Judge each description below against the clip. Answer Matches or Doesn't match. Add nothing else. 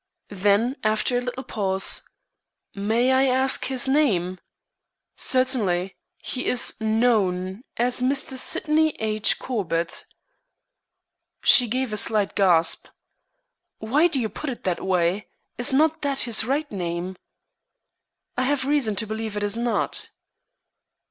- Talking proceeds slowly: Matches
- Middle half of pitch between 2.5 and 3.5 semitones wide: Doesn't match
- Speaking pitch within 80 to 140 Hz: Doesn't match